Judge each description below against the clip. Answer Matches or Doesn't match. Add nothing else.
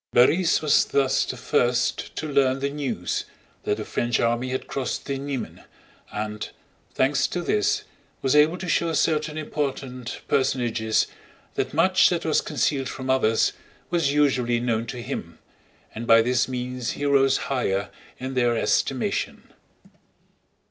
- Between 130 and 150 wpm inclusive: Matches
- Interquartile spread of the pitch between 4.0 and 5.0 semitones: Doesn't match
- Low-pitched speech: Matches